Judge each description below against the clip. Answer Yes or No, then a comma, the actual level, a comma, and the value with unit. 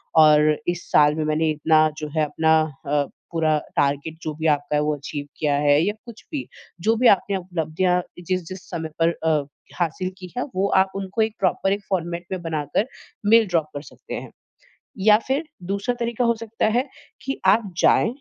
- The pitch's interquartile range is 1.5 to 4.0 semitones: No, average, 4.7 semitones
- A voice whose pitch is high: No, medium, 170 Hz